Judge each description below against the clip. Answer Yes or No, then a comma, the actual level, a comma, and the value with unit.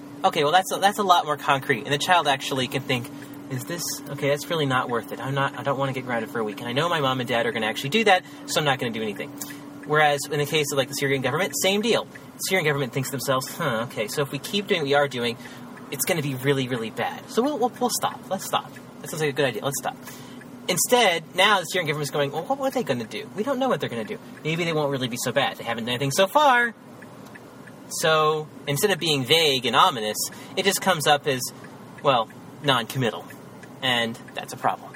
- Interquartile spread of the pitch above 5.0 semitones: Yes, wide, 5.6 semitones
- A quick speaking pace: Yes, fast, 270 wpm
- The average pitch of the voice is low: No, medium, 145 Hz